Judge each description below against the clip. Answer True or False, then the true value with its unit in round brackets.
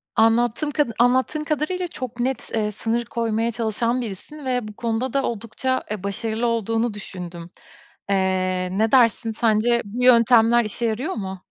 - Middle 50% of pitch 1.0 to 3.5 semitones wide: True (2.7 semitones)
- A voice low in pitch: False (230 Hz)